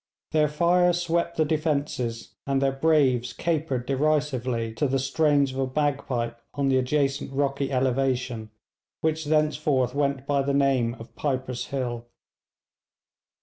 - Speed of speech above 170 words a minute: No, slow, 135 wpm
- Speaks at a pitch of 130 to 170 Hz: Yes, medium, 140 Hz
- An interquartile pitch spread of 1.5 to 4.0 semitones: Yes, average, 2.8 semitones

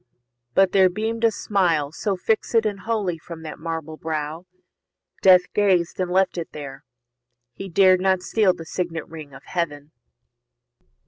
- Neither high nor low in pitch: Yes, medium, 180 Hz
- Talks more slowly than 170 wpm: Yes, average, 150 wpm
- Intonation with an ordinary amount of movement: Yes, average, 3.3 semitones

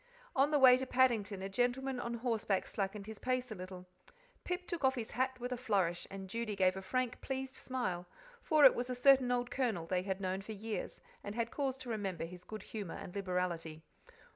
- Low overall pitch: No, high, 225 Hz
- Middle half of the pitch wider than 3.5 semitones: Yes, average, 5.1 semitones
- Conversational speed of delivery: No, fast, 210 wpm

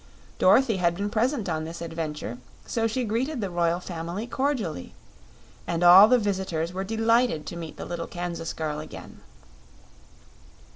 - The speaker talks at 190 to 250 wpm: No, average, 150 wpm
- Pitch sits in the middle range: Yes, medium, 180 Hz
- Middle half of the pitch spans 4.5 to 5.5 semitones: Yes, average, 5.2 semitones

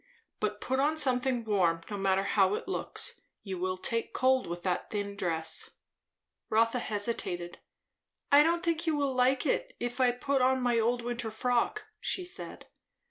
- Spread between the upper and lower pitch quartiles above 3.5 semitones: Yes, average, 4.7 semitones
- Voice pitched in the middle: No, high, 240 Hz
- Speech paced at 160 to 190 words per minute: Yes, average, 170 wpm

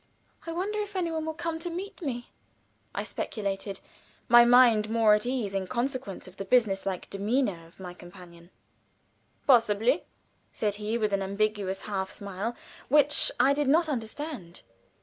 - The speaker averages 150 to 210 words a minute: Yes, average, 160 wpm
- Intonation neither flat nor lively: No, wide, 6.0 semitones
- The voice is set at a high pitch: Yes, high, 225 Hz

